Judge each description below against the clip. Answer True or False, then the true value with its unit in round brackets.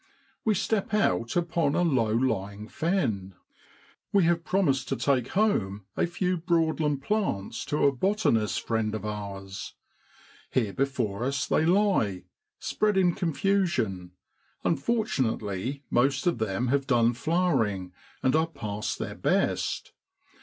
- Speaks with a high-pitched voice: False (135 Hz)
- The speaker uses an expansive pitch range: True (8.4 semitones)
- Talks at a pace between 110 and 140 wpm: True (135 wpm)